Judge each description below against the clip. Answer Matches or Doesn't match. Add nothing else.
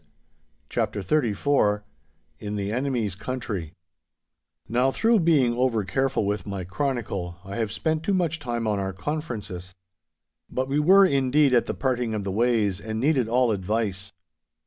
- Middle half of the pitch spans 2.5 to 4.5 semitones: Doesn't match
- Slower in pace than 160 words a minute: Matches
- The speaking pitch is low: Matches